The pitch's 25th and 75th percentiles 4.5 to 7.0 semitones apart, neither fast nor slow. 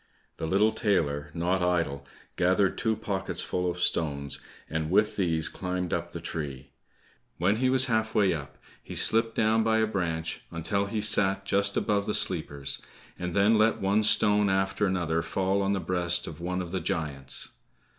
No: average, 3.8 semitones; average, 175 wpm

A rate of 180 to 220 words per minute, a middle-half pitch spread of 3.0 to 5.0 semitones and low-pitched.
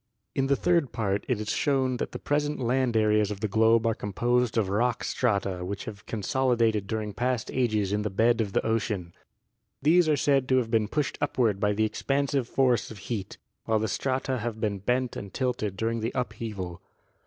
Yes: average, 200 wpm; average, 3.5 semitones; low, 115 Hz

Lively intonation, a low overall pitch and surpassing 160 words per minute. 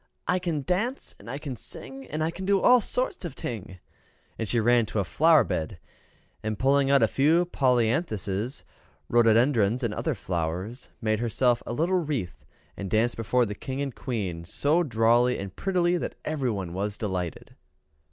Yes: wide, 6.3 semitones; low, 120 Hz; average, 170 wpm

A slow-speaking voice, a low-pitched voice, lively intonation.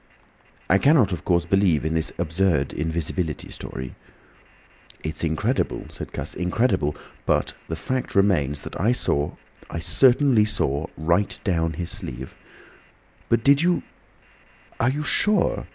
Yes: slow, 120 wpm; very low, 85 Hz; wide, 6.2 semitones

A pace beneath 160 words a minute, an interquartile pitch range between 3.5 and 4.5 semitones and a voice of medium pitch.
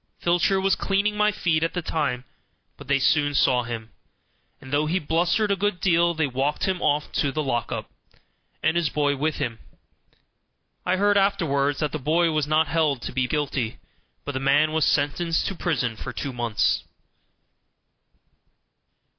No: average, 170 wpm; average, 4.0 semitones; medium, 155 Hz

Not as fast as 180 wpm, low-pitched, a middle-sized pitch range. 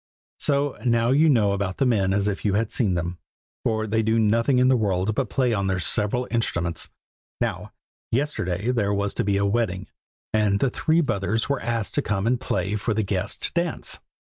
No: fast, 205 wpm; low, 110 Hz; average, 3.7 semitones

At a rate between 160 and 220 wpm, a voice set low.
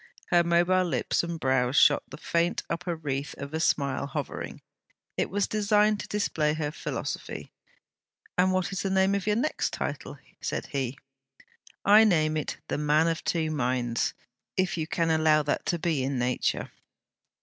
No: average, 165 wpm; medium, 160 Hz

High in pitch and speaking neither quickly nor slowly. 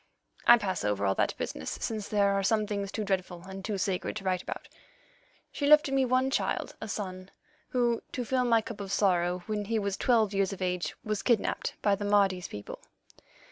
No: high, 200 Hz; fast, 210 wpm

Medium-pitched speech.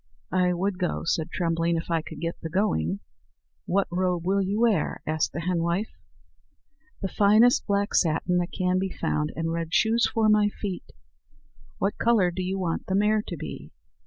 Yes: medium, 180 Hz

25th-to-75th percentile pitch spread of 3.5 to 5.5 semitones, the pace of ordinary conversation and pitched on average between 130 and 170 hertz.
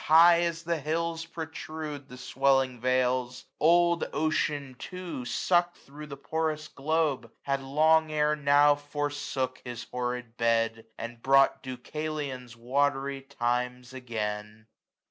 No: average, 3.8 semitones; slow, 120 wpm; medium, 140 Hz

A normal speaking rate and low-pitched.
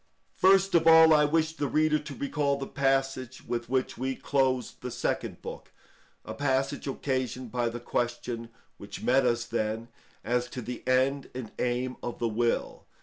Yes: average, 165 wpm; low, 130 Hz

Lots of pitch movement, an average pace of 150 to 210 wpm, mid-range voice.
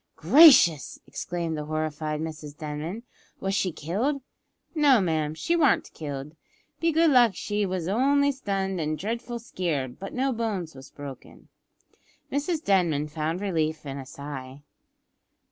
No: wide, 7.5 semitones; average, 140 wpm; medium, 175 Hz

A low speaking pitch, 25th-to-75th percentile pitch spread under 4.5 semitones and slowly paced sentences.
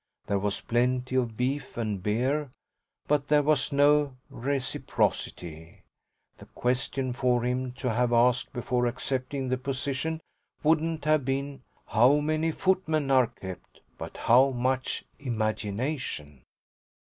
Yes: low, 130 Hz; average, 3.0 semitones; slow, 125 wpm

